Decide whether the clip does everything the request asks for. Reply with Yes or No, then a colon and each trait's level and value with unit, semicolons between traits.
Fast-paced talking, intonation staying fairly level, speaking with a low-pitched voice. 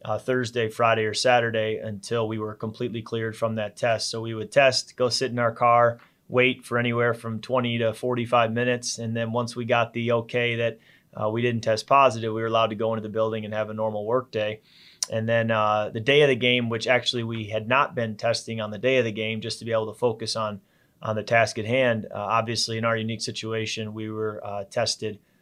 Yes: fast, 235 wpm; narrow, 1.6 semitones; low, 115 Hz